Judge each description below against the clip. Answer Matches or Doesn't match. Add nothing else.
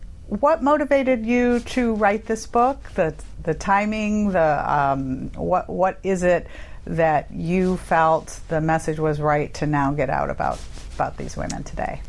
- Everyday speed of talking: Matches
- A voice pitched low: Doesn't match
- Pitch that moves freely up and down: Matches